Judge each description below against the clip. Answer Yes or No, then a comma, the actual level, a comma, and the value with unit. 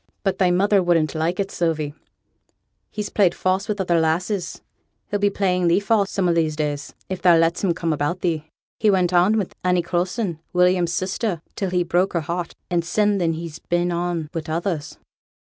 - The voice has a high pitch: No, medium, 175 Hz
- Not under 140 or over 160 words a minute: No, average, 195 wpm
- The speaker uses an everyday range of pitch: No, narrow, 2.3 semitones